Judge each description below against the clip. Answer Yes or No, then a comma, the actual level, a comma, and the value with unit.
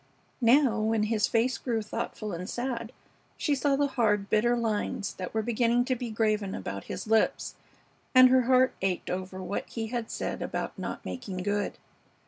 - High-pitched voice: Yes, high, 225 Hz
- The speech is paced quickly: No, average, 175 wpm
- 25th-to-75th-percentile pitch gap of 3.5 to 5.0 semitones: No, average, 2.9 semitones